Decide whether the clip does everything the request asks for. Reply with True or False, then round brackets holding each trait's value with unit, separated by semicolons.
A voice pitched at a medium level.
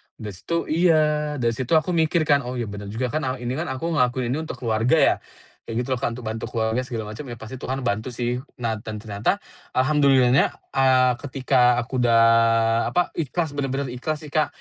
False (130 Hz)